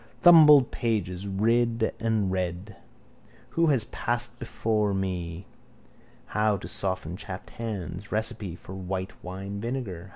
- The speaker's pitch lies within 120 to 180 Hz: No, low, 100 Hz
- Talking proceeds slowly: Yes, slow, 125 wpm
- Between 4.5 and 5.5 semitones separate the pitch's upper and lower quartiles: No, average, 3.8 semitones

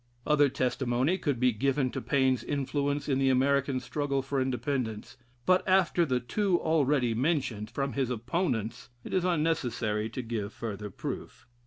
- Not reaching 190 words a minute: Yes, average, 155 wpm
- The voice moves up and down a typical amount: Yes, average, 3.3 semitones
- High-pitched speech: No, low, 135 Hz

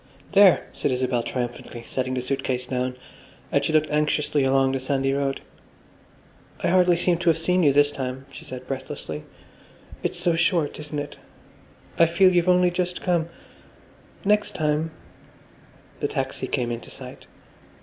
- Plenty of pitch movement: No, average, 4.9 semitones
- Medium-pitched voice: Yes, medium, 150 Hz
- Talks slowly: No, average, 160 wpm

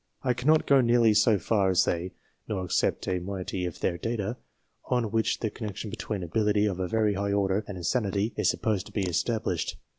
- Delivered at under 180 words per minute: No, average, 200 wpm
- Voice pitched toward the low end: Yes, low, 105 Hz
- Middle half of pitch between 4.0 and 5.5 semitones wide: No, average, 3.2 semitones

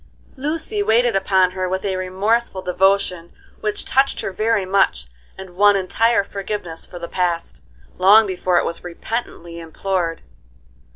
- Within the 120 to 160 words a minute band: Yes, average, 140 wpm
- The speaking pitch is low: No, high, 190 Hz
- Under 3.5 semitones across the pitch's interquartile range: Yes, average, 3.1 semitones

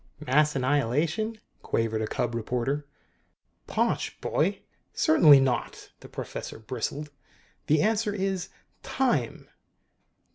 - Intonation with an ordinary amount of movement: No, wide, 5.9 semitones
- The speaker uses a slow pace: Yes, slow, 100 wpm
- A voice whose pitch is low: No, medium, 145 Hz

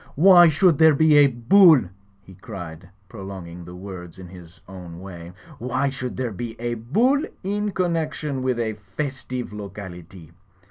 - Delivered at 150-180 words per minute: Yes, average, 155 wpm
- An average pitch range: No, wide, 8.5 semitones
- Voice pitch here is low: Yes, low, 120 Hz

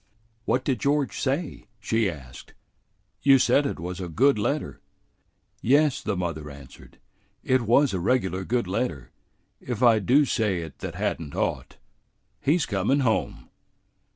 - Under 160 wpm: Yes, average, 150 wpm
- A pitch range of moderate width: No, wide, 6.8 semitones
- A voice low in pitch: Yes, low, 115 Hz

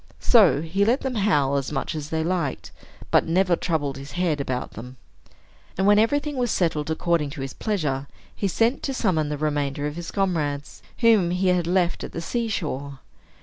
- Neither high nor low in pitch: Yes, medium, 165 Hz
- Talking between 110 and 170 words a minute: No, average, 190 wpm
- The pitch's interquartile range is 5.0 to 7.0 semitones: Yes, average, 5.3 semitones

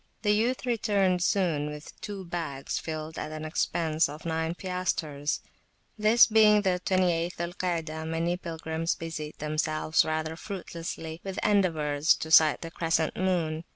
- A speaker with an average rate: Yes, average, 150 wpm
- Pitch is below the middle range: No, medium, 165 Hz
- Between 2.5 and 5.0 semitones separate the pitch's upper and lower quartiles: Yes, average, 2.8 semitones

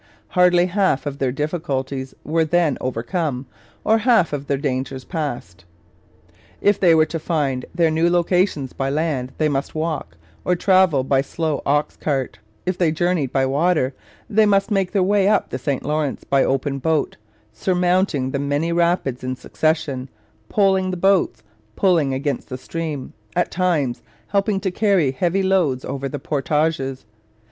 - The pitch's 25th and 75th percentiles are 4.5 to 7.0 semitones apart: Yes, average, 4.9 semitones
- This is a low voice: No, medium, 155 Hz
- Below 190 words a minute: Yes, average, 160 wpm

